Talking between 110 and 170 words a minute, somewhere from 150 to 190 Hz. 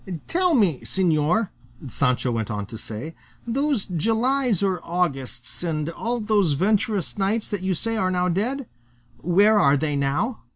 Yes: average, 155 wpm; medium, 185 Hz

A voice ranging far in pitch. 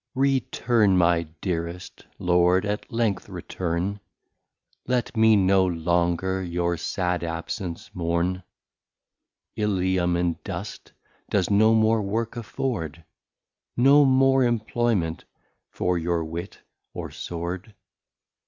No: average, 4.3 semitones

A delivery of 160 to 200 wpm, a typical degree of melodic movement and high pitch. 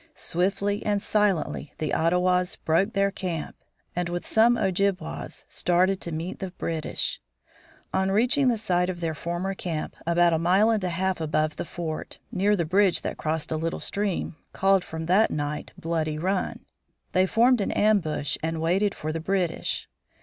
No: average, 170 wpm; average, 3.3 semitones; medium, 180 Hz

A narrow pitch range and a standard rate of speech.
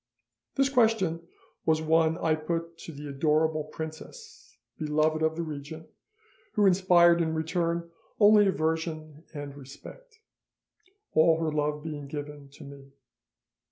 No: narrow, 2.1 semitones; slow, 125 wpm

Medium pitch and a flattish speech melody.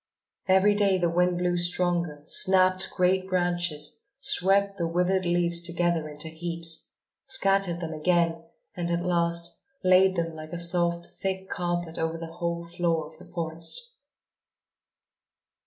Yes: medium, 175 Hz; narrow, 1.7 semitones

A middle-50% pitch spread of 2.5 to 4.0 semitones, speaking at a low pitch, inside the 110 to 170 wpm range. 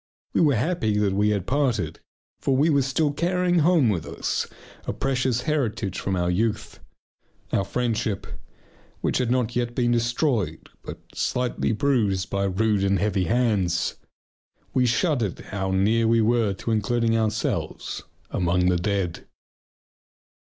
No: average, 4.4 semitones; low, 115 Hz; average, 145 wpm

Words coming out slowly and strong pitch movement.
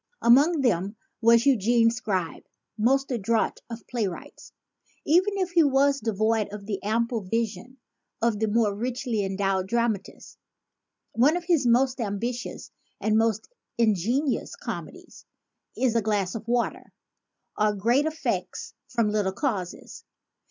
No: slow, 130 wpm; average, 3.6 semitones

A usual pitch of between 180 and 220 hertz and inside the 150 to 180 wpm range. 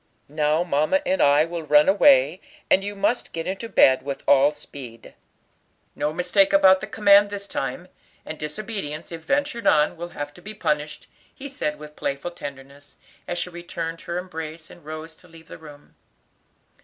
No: medium, 165 Hz; average, 175 wpm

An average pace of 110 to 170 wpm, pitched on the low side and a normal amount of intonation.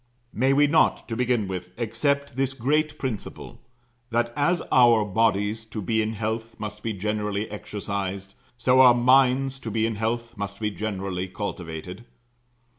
Yes: average, 155 wpm; low, 110 Hz; average, 3.5 semitones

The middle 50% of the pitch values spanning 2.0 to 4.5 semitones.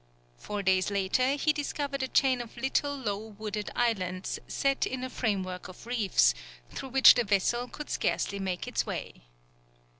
No: average, 5.0 semitones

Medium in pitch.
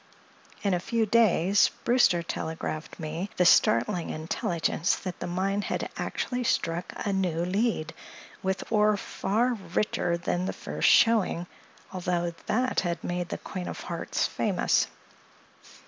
Yes: medium, 180 Hz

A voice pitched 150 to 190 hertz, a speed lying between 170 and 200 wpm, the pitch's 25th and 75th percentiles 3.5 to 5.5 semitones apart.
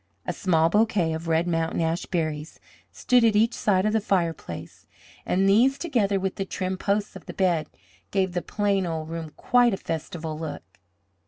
Yes: medium, 185 Hz; average, 180 wpm; average, 4.1 semitones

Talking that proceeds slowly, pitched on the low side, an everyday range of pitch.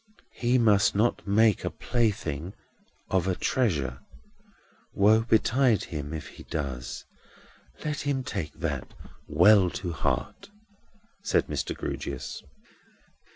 No: slow, 110 wpm; low, 100 Hz; wide, 6.7 semitones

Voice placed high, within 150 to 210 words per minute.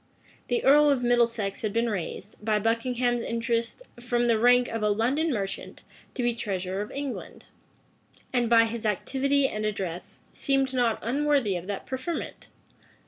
Yes: high, 235 Hz; average, 155 wpm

